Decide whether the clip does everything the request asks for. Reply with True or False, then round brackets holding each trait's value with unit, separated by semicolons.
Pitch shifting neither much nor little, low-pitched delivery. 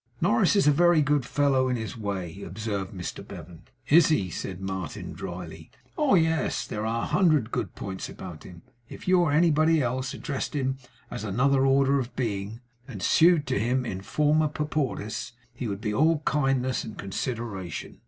False (7.0 semitones; 125 Hz)